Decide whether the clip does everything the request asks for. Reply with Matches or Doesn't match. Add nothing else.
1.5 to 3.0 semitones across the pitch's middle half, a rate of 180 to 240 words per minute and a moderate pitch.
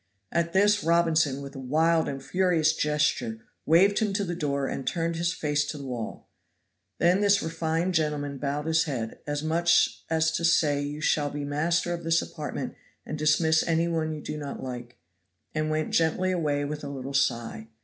Matches